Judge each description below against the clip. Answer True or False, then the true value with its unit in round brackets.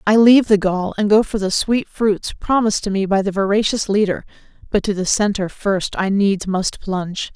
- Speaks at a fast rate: True (210 wpm)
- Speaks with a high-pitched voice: True (200 Hz)